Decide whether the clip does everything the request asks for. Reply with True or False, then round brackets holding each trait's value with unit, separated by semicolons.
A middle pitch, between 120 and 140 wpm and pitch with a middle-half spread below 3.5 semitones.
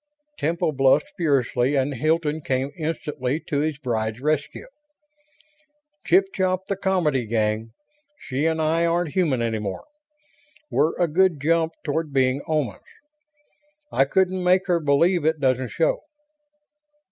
False (150 Hz; 135 wpm; 4.3 semitones)